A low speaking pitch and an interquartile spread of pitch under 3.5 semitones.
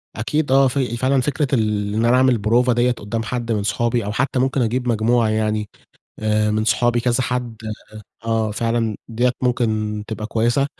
Yes: low, 115 Hz; narrow, 2.5 semitones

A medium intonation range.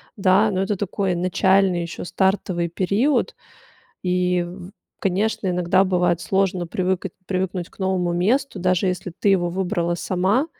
No: narrow, 1.6 semitones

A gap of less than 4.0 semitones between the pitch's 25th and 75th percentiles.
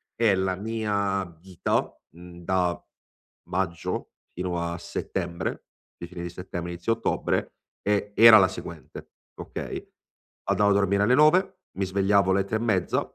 Yes: average, 2.9 semitones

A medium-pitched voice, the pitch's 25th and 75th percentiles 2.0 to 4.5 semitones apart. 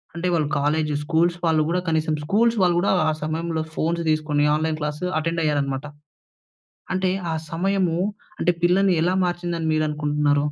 Yes: medium, 160 Hz; narrow, 2.5 semitones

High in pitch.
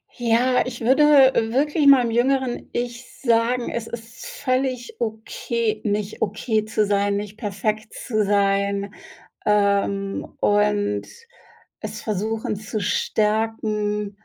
Yes: high, 220 Hz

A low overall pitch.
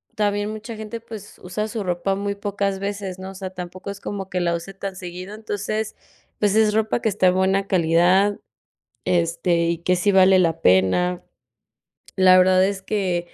No: high, 190 Hz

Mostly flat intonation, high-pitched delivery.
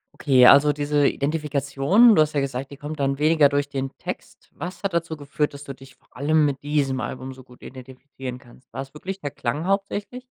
No: narrow, 2.3 semitones; medium, 145 Hz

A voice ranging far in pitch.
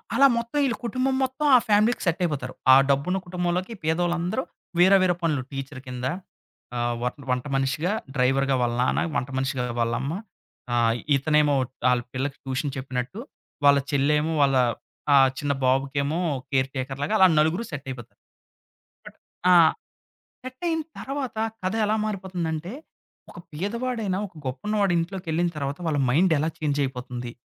Yes: wide, 5.9 semitones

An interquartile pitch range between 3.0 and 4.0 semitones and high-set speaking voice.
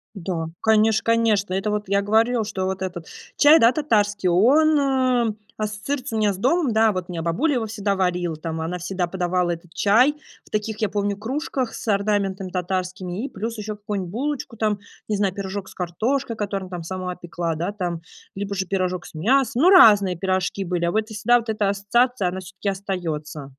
Yes: average, 3.6 semitones; high, 200 Hz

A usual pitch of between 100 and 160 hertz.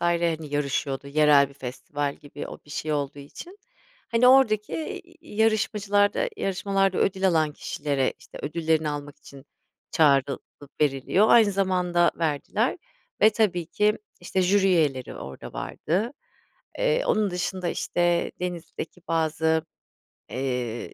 No: medium, 170 Hz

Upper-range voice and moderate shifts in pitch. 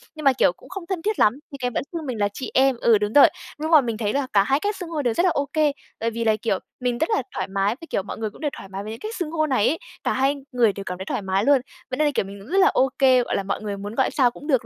No: very high, 255 Hz; wide, 6.5 semitones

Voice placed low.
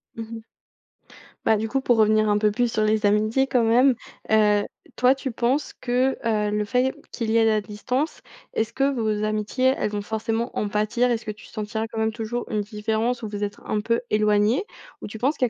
No: high, 220 Hz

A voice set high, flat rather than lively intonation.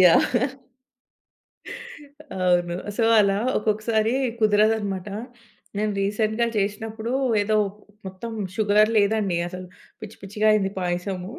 Yes: high, 210 Hz; narrow, 2.3 semitones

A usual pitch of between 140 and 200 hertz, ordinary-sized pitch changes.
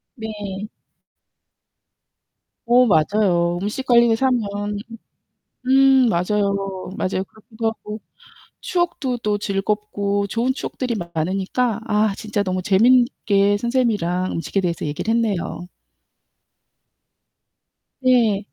No: high, 210 Hz; average, 3.4 semitones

